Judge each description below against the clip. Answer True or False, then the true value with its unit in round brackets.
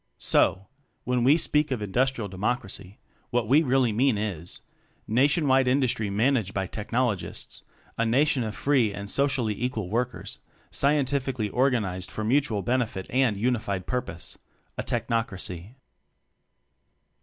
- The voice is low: True (120 Hz)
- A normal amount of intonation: True (4.3 semitones)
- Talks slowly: True (130 wpm)